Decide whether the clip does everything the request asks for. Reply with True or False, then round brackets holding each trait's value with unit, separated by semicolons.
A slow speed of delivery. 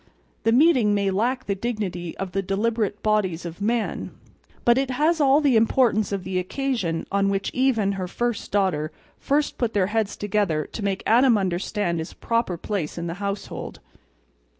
False (175 wpm)